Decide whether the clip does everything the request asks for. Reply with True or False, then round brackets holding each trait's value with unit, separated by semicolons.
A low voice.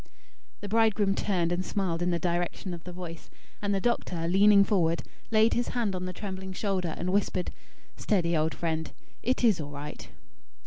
False (185 Hz)